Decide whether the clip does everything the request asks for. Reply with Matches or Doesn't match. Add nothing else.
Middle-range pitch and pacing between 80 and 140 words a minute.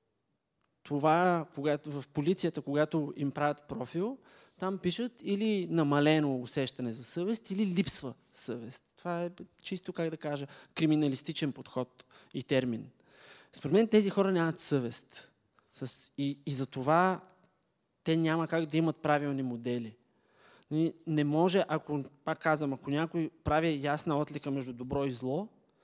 Matches